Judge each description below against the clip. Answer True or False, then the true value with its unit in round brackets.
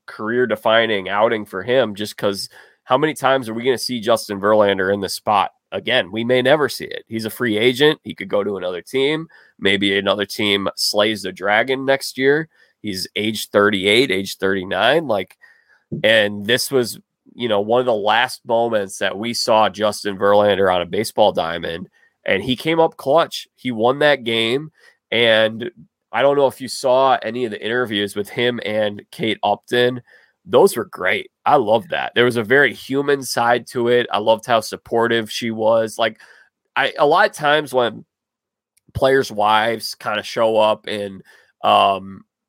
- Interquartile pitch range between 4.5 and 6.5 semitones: False (3.6 semitones)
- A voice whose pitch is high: False (115 Hz)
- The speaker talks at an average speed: True (180 wpm)